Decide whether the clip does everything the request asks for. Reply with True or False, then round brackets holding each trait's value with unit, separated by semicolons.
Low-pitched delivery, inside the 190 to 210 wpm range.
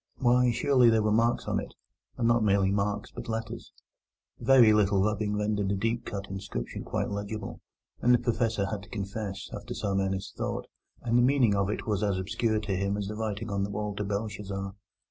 True (105 Hz; 205 wpm)